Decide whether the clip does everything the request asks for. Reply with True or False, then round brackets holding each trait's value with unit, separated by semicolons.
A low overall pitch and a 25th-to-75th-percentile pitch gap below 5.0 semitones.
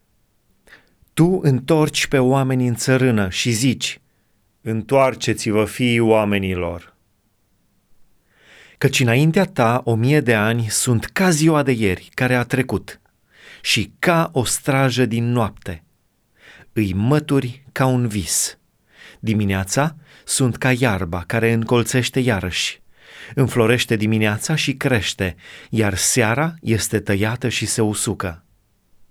True (115 Hz; 4.2 semitones)